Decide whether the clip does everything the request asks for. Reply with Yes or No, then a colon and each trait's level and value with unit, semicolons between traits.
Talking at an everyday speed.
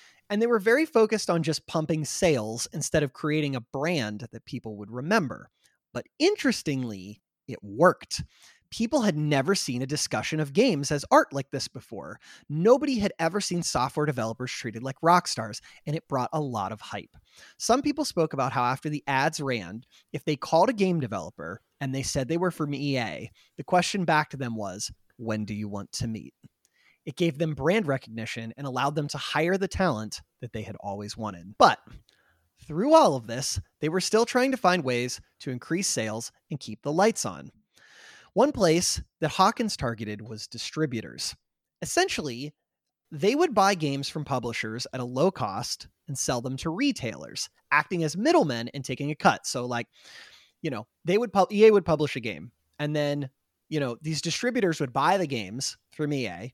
Yes: average, 185 wpm